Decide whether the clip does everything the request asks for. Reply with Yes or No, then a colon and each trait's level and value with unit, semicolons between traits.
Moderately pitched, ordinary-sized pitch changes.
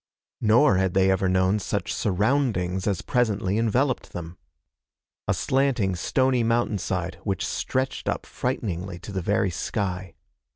No: low, 100 Hz; average, 4.5 semitones